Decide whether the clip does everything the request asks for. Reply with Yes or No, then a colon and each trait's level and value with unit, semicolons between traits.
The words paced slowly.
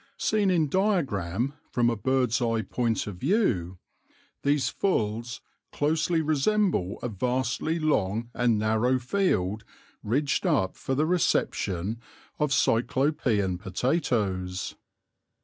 Yes: slow, 110 wpm